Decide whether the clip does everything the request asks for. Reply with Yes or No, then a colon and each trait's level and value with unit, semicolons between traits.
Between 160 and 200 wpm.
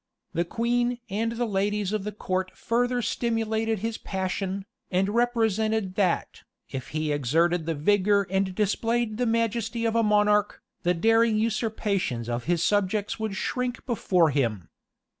No: average, 145 wpm